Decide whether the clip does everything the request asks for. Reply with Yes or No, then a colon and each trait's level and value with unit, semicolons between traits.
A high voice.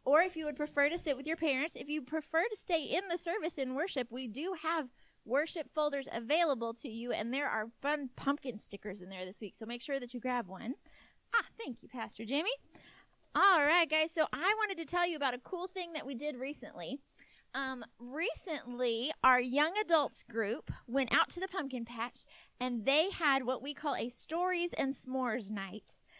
Yes: very high, 280 Hz